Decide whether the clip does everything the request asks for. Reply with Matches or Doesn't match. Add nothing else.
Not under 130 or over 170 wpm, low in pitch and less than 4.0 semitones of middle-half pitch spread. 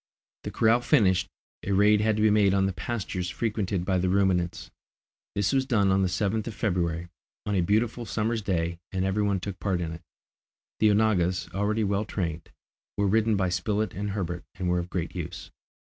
Doesn't match